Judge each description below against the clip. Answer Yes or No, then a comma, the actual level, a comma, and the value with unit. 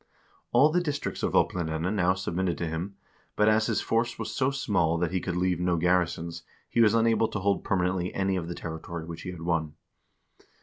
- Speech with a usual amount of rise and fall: Yes, average, 3.9 semitones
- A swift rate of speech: Yes, fast, 210 wpm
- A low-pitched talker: Yes, very low, 90 Hz